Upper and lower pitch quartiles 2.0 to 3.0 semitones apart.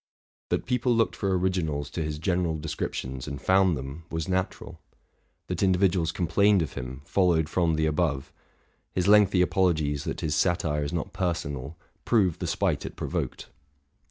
No: average, 3.8 semitones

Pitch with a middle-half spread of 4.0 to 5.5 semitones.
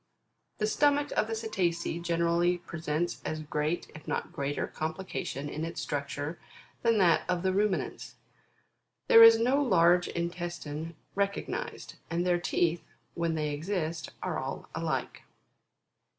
No: average, 3.3 semitones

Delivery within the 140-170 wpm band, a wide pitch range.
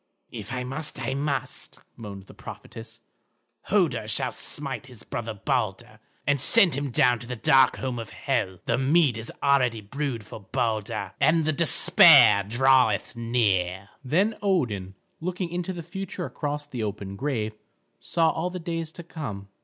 Yes: average, 160 wpm; wide, 5.8 semitones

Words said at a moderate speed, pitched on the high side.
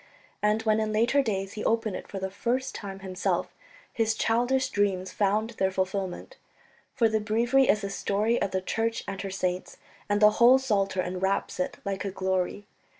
Yes: average, 185 wpm; high, 205 Hz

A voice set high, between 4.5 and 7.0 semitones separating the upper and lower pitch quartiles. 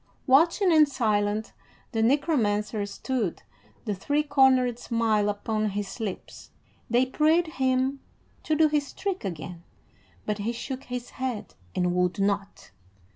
Yes: high, 235 Hz; average, 5.3 semitones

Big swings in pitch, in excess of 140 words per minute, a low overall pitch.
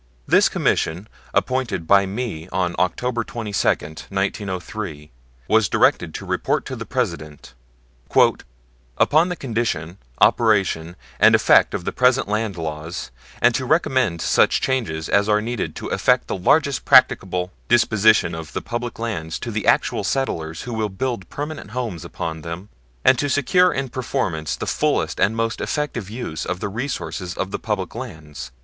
Yes: wide, 6.1 semitones; average, 155 wpm; low, 105 Hz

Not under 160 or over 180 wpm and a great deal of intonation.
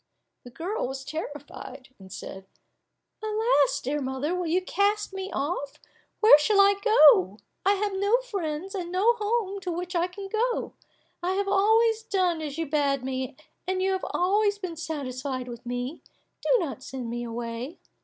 Yes: average, 170 wpm; wide, 6.9 semitones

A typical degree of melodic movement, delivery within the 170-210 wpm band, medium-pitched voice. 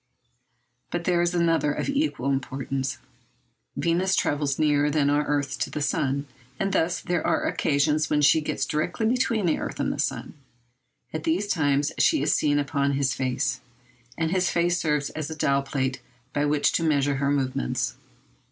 Yes: average, 3.3 semitones; average, 175 wpm; medium, 150 Hz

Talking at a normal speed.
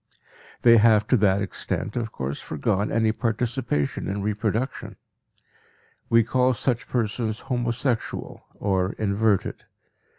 No: slow, 110 wpm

